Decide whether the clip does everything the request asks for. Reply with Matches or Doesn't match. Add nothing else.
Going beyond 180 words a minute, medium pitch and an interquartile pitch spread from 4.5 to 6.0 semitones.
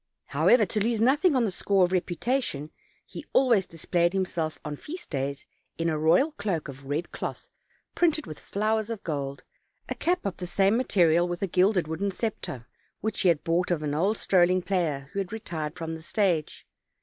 Matches